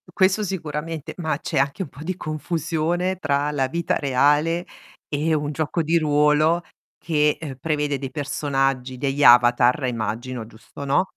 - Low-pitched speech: No, medium, 150 Hz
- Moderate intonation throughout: Yes, average, 3.1 semitones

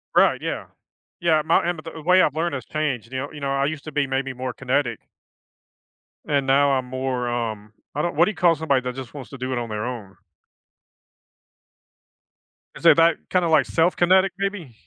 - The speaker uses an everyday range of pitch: Yes, average, 4.3 semitones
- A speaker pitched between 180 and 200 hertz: No, medium, 140 Hz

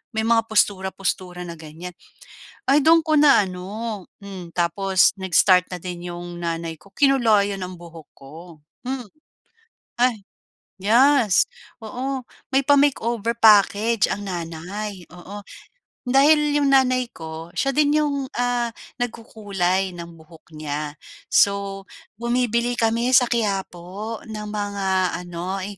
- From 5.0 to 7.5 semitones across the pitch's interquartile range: Yes, average, 5.3 semitones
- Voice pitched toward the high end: Yes, high, 200 Hz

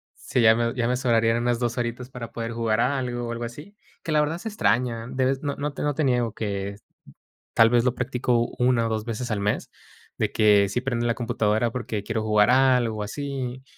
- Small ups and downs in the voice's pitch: Yes, narrow, 2.2 semitones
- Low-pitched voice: Yes, low, 120 Hz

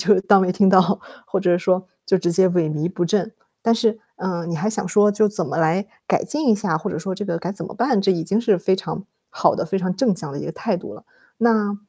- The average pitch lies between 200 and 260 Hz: No, high, 190 Hz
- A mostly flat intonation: No, average, 3.0 semitones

